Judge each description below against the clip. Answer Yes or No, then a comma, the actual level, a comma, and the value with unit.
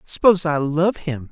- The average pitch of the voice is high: No, medium, 160 Hz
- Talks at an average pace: Yes, average, 185 wpm